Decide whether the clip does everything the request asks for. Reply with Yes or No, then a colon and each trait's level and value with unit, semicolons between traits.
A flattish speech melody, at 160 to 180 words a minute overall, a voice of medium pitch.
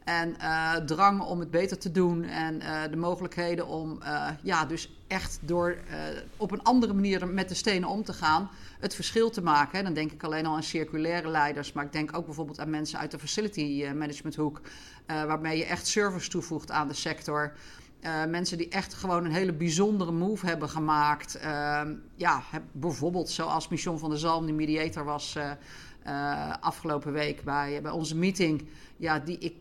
No: narrow, 2.3 semitones; average, 195 wpm; medium, 160 Hz